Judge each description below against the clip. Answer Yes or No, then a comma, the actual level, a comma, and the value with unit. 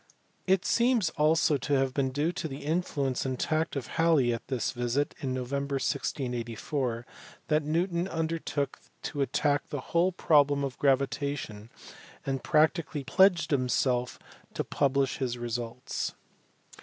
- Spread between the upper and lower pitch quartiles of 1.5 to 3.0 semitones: No, average, 3.6 semitones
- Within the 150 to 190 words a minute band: No, average, 140 wpm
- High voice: No, medium, 140 Hz